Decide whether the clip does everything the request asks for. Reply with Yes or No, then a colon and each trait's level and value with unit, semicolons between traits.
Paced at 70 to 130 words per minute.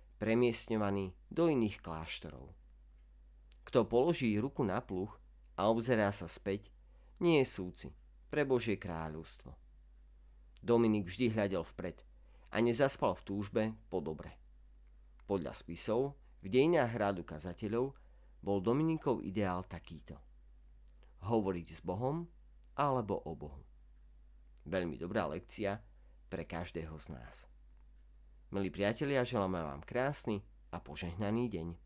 Yes: average, 115 wpm